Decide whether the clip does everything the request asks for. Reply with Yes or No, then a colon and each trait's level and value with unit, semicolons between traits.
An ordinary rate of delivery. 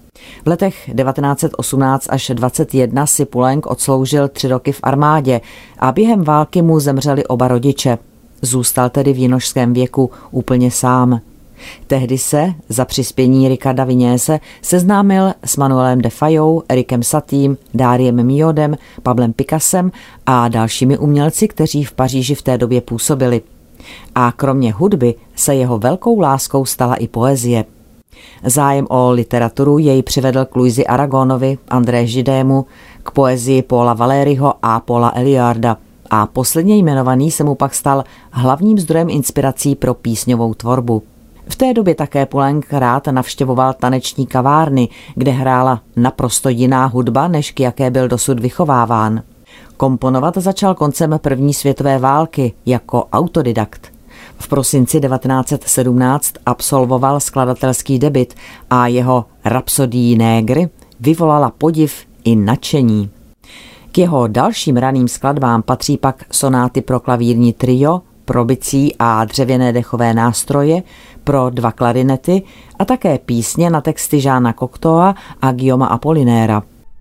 Yes: average, 130 wpm